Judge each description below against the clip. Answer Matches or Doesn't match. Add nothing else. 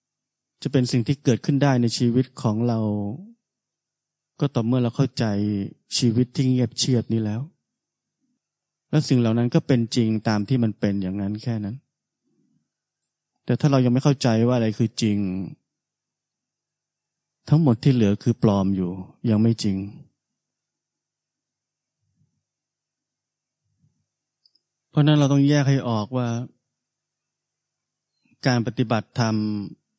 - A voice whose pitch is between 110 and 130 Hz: Matches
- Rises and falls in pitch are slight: Doesn't match